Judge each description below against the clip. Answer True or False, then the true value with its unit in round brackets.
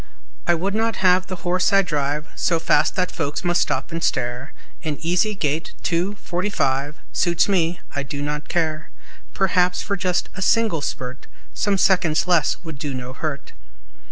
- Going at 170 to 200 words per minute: True (175 wpm)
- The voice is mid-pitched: True (170 Hz)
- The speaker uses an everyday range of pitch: True (3.7 semitones)